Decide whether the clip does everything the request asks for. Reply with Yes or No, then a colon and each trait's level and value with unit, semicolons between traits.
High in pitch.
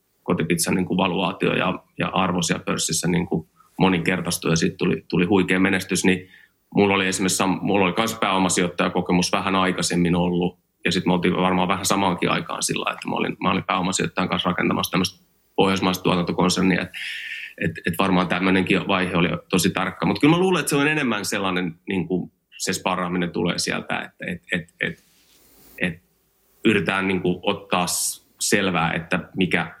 No: very low, 90 Hz